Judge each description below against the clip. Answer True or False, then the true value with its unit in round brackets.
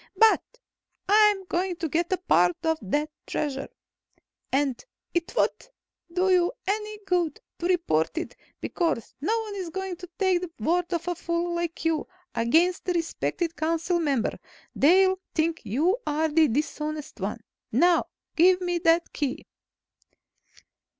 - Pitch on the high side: True (340 Hz)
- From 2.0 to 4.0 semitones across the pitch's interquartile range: True (2.8 semitones)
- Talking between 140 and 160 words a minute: True (145 wpm)